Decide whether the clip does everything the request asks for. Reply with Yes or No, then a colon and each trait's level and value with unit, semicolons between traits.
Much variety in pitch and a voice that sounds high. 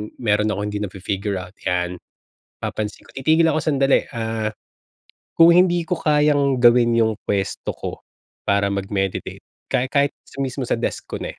No: wide, 5.8 semitones; low, 115 Hz